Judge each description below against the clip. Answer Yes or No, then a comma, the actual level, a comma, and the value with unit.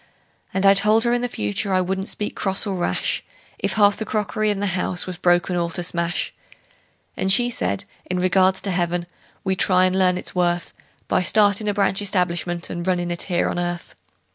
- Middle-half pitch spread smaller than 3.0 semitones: Yes, narrow, 2.4 semitones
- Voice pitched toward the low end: No, medium, 185 Hz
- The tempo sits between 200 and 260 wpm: Yes, fast, 205 wpm